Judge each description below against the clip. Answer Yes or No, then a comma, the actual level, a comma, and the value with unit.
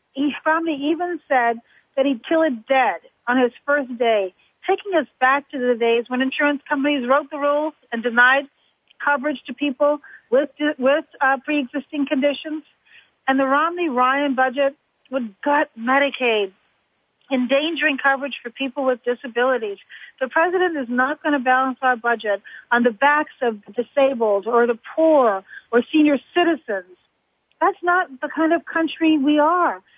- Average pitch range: Yes, average, 3.3 semitones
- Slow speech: No, average, 150 wpm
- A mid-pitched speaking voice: No, very high, 275 Hz